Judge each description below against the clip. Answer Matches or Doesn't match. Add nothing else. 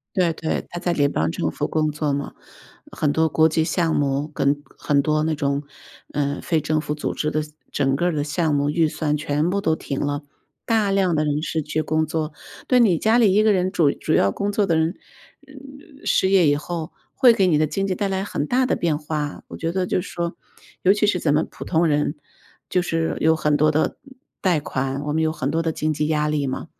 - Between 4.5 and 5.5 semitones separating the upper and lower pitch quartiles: Doesn't match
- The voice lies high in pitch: Doesn't match